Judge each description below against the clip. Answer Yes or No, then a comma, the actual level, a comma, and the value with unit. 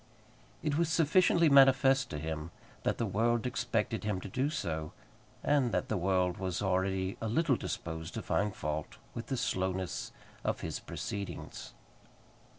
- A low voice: Yes, low, 105 Hz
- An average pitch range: No, wide, 6.4 semitones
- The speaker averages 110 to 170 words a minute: Yes, average, 155 wpm